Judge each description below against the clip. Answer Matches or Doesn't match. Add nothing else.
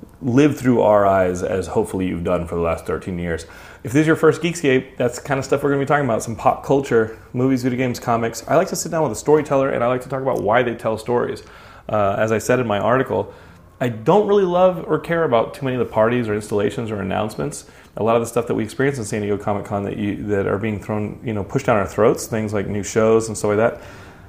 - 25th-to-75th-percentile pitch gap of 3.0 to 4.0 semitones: Doesn't match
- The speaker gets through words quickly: Matches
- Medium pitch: Doesn't match